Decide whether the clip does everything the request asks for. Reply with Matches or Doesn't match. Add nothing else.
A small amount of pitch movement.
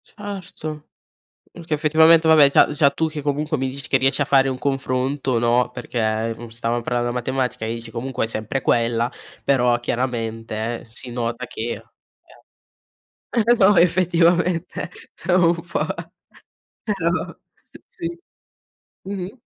Doesn't match